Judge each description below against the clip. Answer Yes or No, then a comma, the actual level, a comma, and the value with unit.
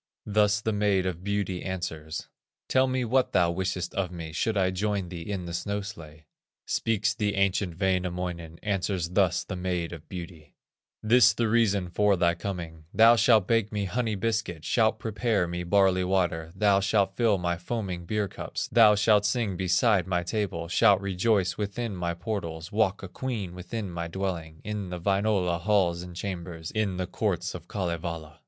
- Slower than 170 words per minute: No, average, 175 wpm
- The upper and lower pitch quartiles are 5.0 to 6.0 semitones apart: No, average, 3.2 semitones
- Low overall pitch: Yes, very low, 95 Hz